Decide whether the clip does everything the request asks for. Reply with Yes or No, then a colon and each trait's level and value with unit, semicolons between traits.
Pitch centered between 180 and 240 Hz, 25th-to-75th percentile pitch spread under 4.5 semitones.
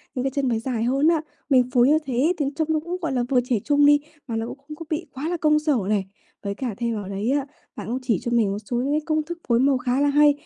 No: very high, 265 Hz; average, 4.1 semitones